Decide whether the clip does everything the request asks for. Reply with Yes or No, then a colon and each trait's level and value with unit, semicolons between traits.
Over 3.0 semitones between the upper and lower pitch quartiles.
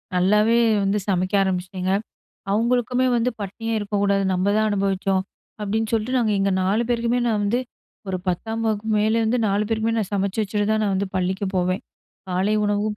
No: narrow, 2.5 semitones